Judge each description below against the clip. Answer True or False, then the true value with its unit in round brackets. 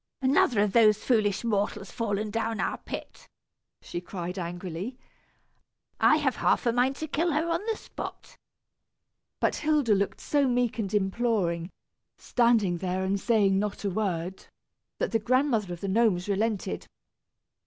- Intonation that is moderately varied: True (4.1 semitones)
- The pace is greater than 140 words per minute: True (150 wpm)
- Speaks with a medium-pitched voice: False (210 Hz)